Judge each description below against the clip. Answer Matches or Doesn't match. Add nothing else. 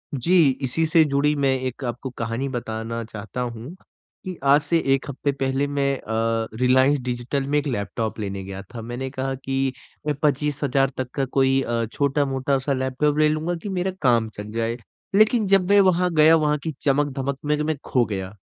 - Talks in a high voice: Doesn't match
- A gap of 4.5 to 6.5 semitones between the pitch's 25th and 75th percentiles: Doesn't match